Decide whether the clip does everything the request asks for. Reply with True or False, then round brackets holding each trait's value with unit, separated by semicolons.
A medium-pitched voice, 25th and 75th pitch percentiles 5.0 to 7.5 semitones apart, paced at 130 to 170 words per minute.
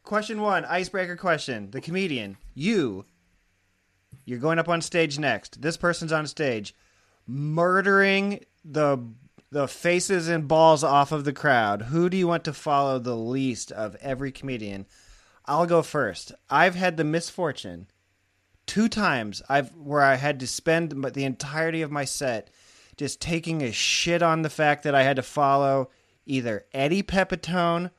True (145 Hz; 5.3 semitones; 155 wpm)